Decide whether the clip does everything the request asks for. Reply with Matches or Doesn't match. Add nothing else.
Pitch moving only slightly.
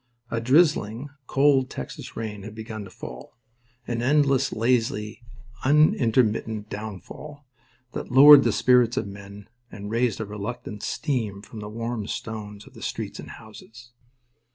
Doesn't match